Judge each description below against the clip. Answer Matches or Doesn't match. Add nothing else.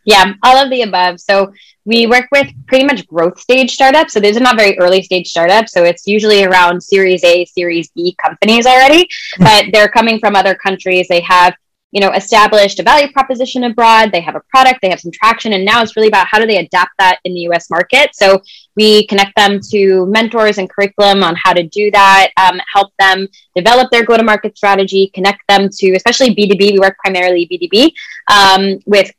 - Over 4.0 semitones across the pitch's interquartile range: Doesn't match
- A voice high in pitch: Matches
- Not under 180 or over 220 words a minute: Matches